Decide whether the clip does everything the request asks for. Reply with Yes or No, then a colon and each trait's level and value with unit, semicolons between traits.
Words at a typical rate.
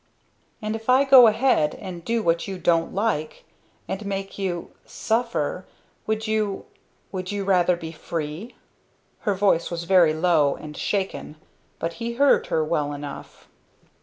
Yes: average, 150 wpm